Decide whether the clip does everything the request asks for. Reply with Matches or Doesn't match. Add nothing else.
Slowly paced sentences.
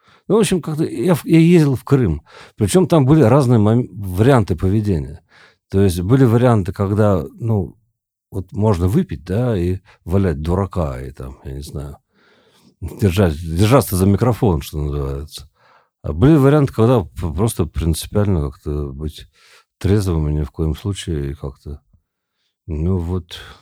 Doesn't match